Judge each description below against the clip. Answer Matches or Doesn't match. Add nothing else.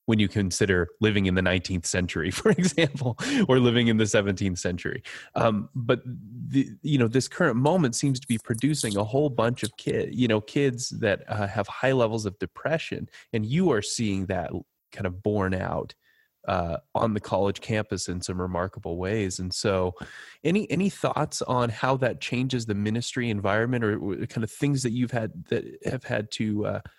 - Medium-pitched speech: Doesn't match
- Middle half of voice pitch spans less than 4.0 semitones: Doesn't match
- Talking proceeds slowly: Doesn't match